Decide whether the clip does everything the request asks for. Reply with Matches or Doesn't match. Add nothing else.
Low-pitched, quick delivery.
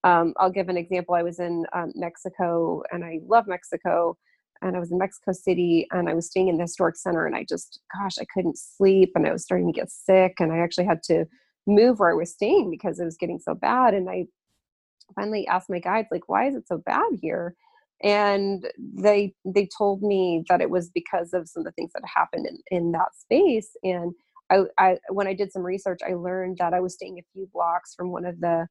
Doesn't match